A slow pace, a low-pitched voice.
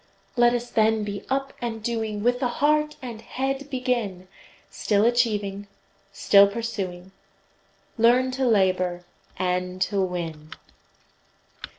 No: slow, 115 wpm; high, 220 Hz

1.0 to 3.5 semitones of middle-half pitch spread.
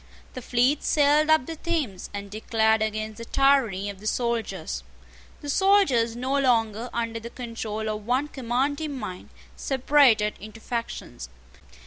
No: average, 4.2 semitones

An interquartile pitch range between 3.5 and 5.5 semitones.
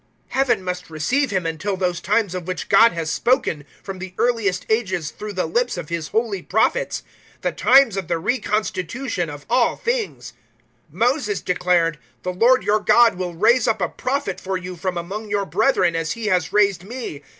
Yes: average, 4.6 semitones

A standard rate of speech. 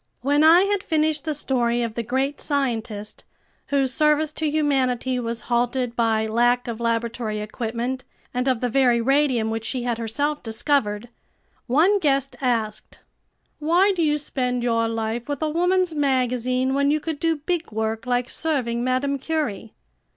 Yes: average, 160 wpm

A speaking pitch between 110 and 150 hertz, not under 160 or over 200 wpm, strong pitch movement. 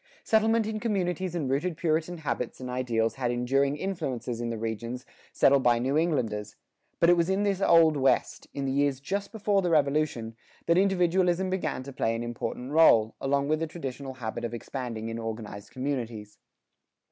Yes: medium, 140 Hz; average, 180 wpm; wide, 6.4 semitones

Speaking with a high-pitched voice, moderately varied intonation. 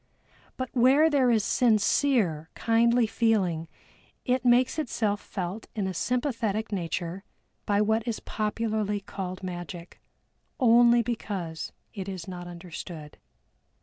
Yes: high, 215 Hz; average, 4.5 semitones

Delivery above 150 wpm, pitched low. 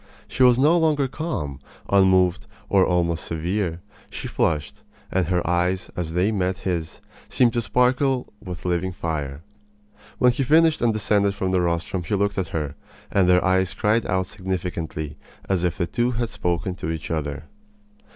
Yes: average, 170 wpm; very low, 95 Hz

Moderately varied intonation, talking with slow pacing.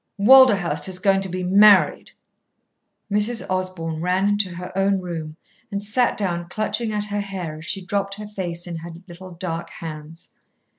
No: average, 3.0 semitones; average, 165 wpm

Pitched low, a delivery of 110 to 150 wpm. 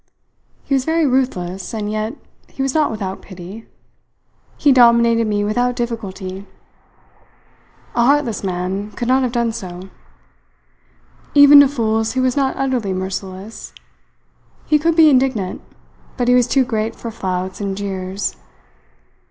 No: high, 225 Hz; average, 140 wpm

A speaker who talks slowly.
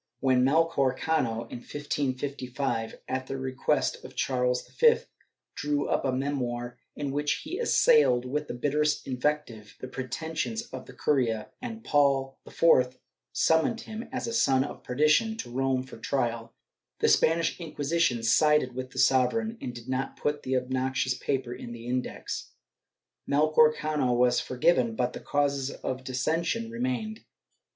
No: average, 150 wpm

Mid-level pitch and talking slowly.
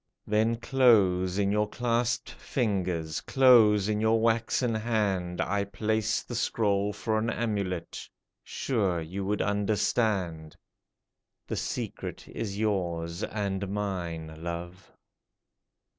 No: low, 105 Hz; slow, 110 wpm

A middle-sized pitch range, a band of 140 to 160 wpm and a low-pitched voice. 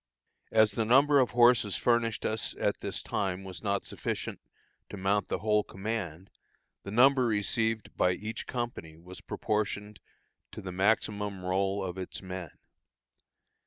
Yes: average, 3.0 semitones; average, 145 wpm; low, 105 Hz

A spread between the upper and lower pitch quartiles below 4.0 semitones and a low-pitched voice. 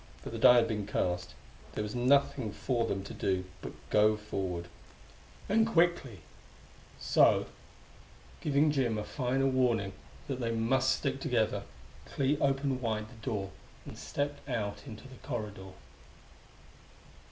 No: average, 4.3 semitones; low, 120 Hz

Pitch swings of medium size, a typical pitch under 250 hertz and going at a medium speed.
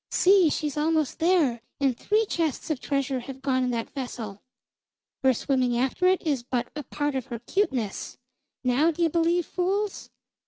No: average, 5.0 semitones; very high, 280 Hz; average, 165 wpm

